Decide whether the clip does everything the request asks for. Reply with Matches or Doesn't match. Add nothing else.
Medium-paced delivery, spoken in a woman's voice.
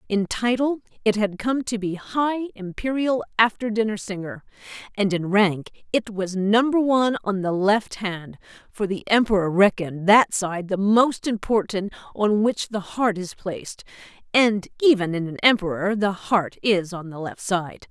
Matches